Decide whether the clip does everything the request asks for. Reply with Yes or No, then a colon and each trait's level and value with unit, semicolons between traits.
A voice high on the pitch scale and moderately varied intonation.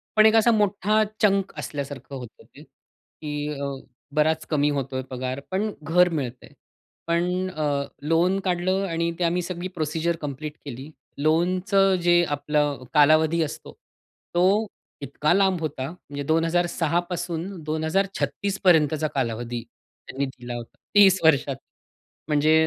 No: medium, 160 Hz; average, 3.9 semitones